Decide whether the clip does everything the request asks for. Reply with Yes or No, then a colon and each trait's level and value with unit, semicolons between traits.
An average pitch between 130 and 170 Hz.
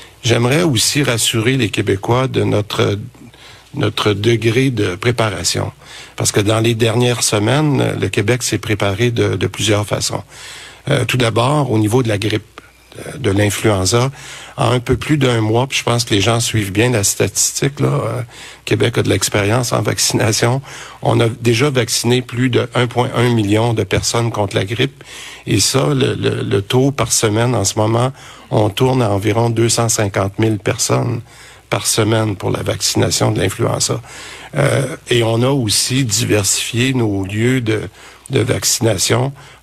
No: low, 115 Hz